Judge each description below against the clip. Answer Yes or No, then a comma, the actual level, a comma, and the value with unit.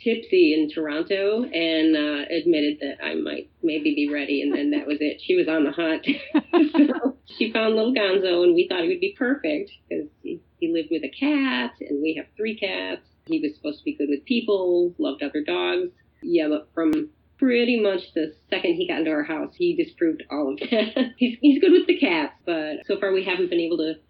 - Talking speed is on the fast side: Yes, fast, 220 wpm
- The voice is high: Yes, high, 200 Hz